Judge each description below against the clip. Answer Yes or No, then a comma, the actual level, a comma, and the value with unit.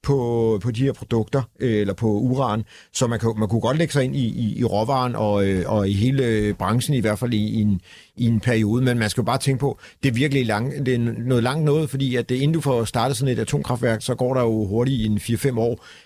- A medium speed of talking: No, fast, 260 wpm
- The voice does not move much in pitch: No, average, 3.2 semitones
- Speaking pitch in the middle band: No, low, 120 Hz